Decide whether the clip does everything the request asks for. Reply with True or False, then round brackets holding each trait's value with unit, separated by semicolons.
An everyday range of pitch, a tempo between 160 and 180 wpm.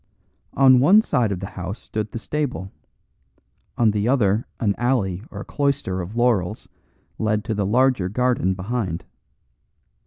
False (4.5 semitones; 145 wpm)